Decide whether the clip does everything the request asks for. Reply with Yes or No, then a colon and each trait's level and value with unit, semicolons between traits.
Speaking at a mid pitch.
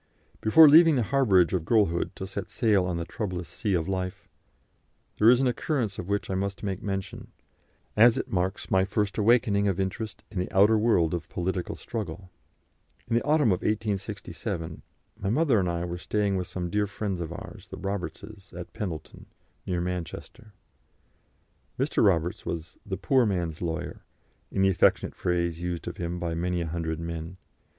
No: very low, 95 Hz